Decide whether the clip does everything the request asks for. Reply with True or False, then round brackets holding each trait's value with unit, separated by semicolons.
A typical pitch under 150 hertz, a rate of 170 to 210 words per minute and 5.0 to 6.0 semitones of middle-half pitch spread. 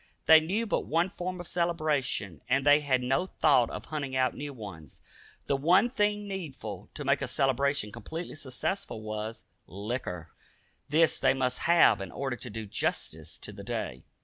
True (140 Hz; 175 wpm; 5.6 semitones)